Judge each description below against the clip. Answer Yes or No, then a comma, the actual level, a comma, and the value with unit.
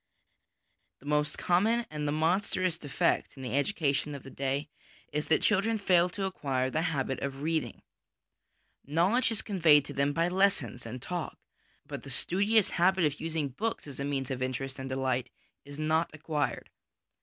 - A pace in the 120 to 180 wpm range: Yes, average, 170 wpm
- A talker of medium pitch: Yes, medium, 150 Hz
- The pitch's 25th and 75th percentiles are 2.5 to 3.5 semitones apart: No, average, 4.6 semitones